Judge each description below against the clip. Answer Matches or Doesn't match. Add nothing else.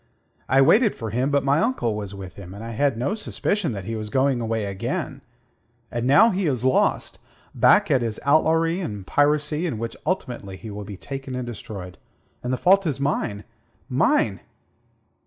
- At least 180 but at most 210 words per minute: Matches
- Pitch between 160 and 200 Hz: Doesn't match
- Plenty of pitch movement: Matches